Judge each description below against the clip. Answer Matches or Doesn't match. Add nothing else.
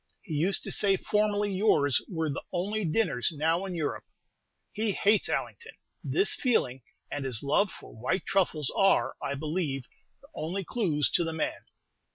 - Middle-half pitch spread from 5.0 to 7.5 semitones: Matches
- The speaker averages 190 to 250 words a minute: Doesn't match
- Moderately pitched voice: Matches